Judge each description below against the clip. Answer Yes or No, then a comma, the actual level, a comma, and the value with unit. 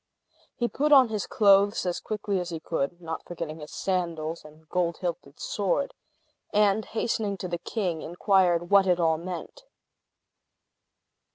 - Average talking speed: Yes, average, 150 wpm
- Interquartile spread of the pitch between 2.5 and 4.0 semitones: Yes, average, 3.5 semitones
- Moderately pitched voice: Yes, medium, 180 Hz